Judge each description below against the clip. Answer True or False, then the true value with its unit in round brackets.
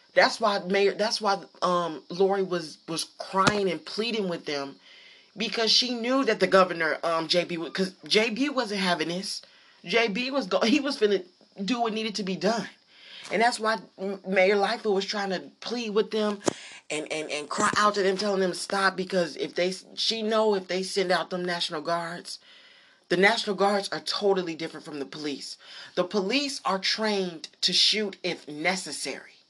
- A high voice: True (195 Hz)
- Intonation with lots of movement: False (3.6 semitones)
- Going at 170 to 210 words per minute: True (190 wpm)